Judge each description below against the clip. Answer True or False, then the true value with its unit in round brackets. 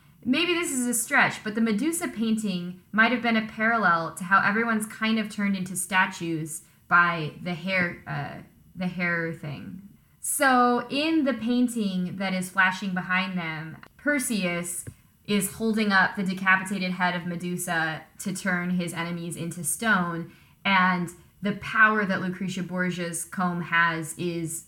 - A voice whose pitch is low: False (185 Hz)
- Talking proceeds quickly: False (150 wpm)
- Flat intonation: False (4.0 semitones)